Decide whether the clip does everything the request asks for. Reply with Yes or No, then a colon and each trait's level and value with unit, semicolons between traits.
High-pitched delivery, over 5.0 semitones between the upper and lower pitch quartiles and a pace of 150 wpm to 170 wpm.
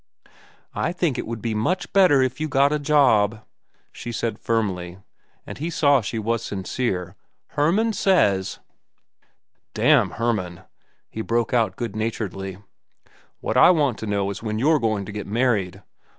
No: low, 115 Hz; wide, 5.6 semitones; average, 155 wpm